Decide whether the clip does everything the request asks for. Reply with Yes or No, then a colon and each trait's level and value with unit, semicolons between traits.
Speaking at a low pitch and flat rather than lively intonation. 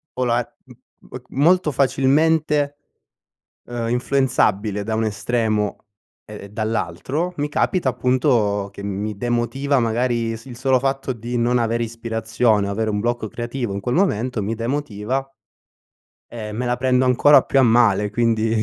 No: low, 120 Hz; average, 3.2 semitones